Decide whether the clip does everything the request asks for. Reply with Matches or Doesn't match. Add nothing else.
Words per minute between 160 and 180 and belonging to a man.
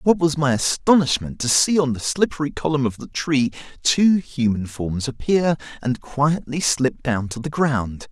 Matches